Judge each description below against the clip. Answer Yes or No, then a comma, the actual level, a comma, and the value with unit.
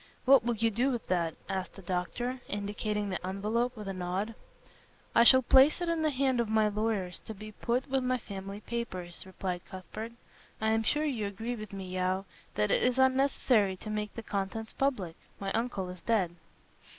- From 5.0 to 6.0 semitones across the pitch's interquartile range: No, average, 4.1 semitones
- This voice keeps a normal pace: Yes, average, 190 wpm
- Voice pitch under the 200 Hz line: No, high, 215 Hz